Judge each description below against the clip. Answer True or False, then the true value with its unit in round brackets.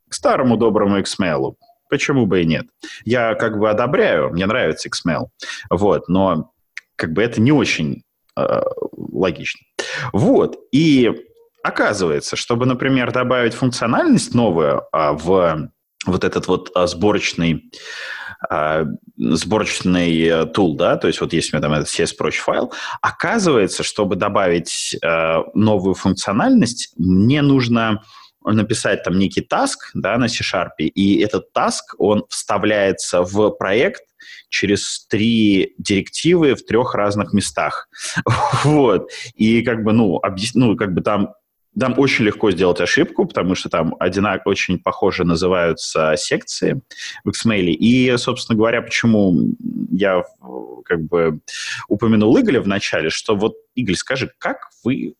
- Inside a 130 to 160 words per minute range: True (135 wpm)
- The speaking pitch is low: True (105 Hz)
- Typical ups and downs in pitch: False (5.7 semitones)